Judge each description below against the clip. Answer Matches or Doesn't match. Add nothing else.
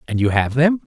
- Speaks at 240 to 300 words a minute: Matches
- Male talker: Matches